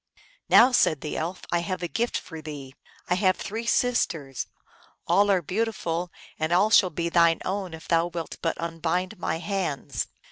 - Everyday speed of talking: Yes, average, 185 wpm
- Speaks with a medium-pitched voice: Yes, medium, 175 Hz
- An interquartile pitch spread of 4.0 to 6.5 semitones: No, average, 3.2 semitones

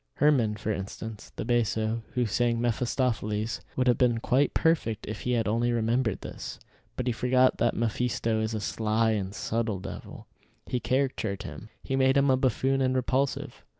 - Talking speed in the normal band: Yes, average, 175 wpm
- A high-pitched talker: No, low, 115 Hz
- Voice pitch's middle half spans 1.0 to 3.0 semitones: Yes, average, 2.7 semitones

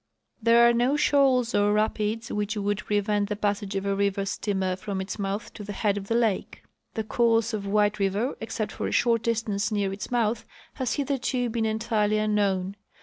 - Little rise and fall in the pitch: Yes, narrow, 2.3 semitones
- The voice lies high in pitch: Yes, high, 210 Hz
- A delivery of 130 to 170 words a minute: No, average, 195 wpm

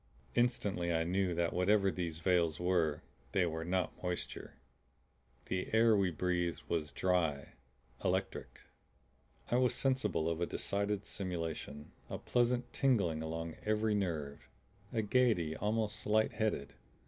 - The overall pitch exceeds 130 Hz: No, very low, 90 Hz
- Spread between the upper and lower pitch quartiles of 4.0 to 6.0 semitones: Yes, average, 4.4 semitones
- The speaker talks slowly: Yes, slow, 130 wpm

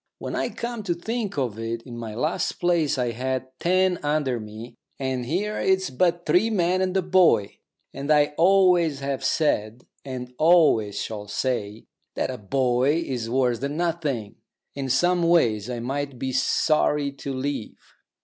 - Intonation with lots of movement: Yes, wide, 5.9 semitones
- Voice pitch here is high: No, medium, 140 Hz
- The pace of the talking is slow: No, average, 165 wpm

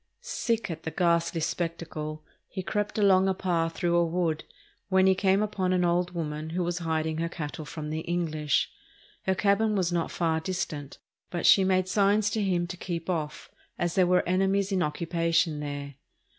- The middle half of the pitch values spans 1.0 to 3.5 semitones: Yes, average, 2.7 semitones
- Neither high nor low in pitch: Yes, medium, 175 Hz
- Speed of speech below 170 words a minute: No, average, 185 wpm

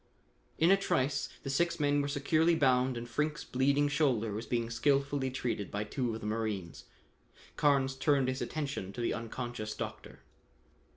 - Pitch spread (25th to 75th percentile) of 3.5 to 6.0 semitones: Yes, average, 3.9 semitones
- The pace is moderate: Yes, average, 165 wpm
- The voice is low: Yes, low, 130 Hz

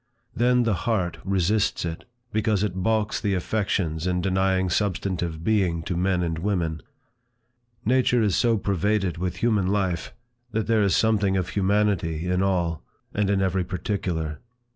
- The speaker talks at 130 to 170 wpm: Yes, average, 150 wpm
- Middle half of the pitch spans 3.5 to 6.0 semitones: No, average, 3.1 semitones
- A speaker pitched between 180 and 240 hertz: No, very low, 95 Hz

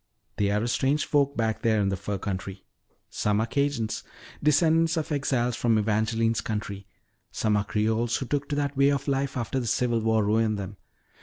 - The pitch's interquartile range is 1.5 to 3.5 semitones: No, average, 4.7 semitones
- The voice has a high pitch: No, low, 115 Hz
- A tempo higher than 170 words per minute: Yes, average, 190 wpm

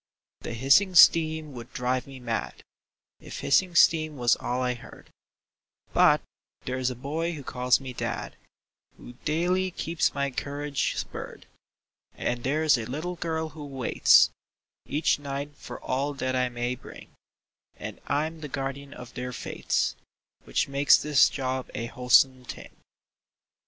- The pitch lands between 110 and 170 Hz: Yes, medium, 140 Hz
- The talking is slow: No, average, 145 wpm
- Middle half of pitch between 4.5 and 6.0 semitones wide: No, average, 3.5 semitones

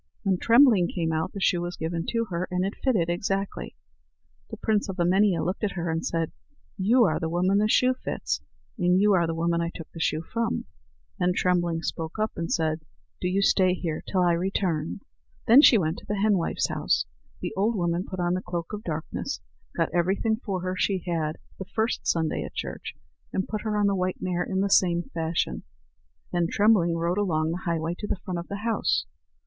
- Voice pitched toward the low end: No, medium, 180 Hz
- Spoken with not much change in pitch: No, average, 3.1 semitones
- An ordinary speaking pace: No, fast, 210 wpm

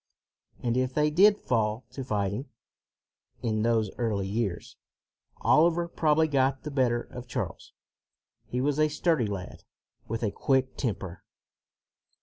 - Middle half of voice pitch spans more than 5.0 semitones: Yes, wide, 5.4 semitones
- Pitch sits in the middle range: No, low, 125 Hz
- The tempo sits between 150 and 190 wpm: No, slow, 135 wpm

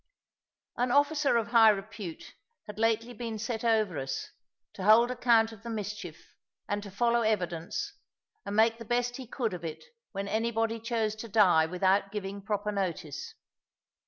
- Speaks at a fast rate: No, average, 160 wpm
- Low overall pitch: No, high, 220 Hz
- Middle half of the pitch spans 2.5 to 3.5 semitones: Yes, average, 2.9 semitones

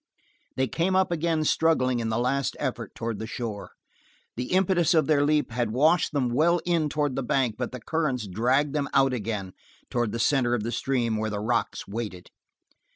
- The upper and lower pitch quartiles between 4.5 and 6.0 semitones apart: Yes, average, 4.9 semitones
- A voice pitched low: Yes, low, 130 Hz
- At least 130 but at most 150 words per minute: No, average, 195 wpm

